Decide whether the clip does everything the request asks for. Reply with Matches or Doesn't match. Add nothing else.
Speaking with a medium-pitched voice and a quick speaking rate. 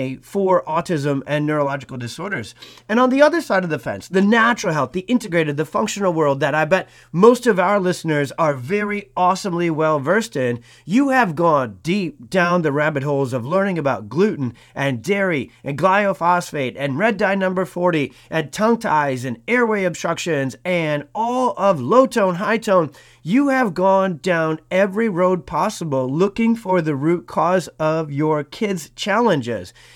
Doesn't match